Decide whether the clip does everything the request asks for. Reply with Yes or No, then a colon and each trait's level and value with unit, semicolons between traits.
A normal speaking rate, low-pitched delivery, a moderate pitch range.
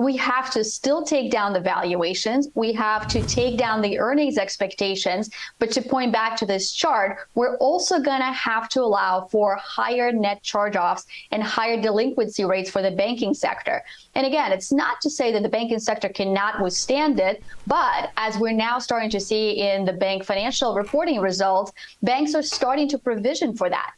No: average, 190 wpm; high, 225 Hz; average, 4.6 semitones